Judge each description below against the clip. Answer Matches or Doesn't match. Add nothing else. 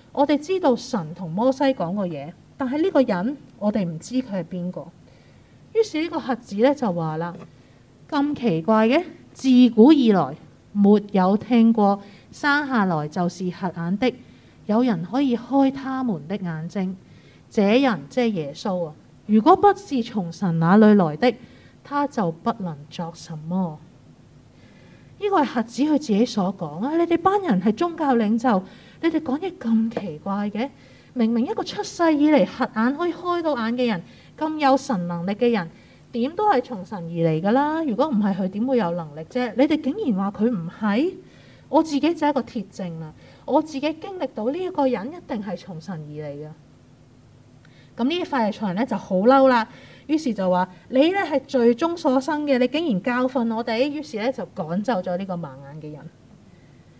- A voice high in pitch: Matches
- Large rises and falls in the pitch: Matches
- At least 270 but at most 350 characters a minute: Doesn't match